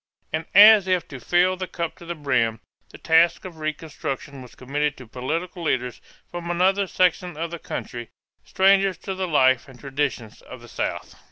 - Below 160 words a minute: No, average, 180 wpm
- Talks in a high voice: No, medium, 160 Hz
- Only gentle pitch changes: No, average, 5.3 semitones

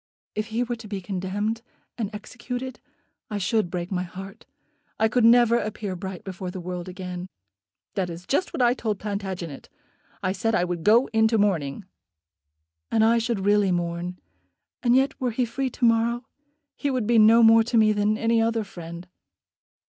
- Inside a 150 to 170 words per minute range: No, average, 180 wpm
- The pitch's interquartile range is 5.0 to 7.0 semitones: No, average, 3.8 semitones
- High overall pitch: Yes, high, 215 Hz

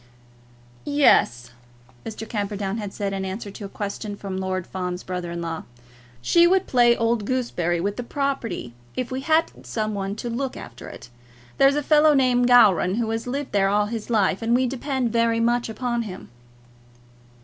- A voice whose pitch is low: No, high, 225 Hz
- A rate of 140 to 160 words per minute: No, average, 180 wpm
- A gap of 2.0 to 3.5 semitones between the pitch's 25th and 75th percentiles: No, average, 4.2 semitones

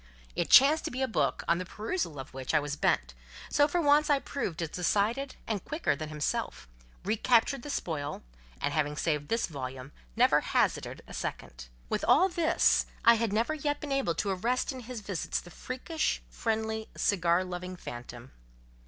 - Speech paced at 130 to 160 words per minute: No, average, 175 wpm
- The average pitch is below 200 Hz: No, high, 205 Hz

